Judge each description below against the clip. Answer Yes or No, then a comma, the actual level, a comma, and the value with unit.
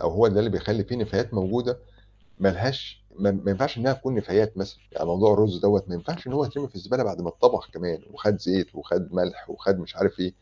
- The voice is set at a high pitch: No, low, 105 Hz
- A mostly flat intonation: No, average, 4.1 semitones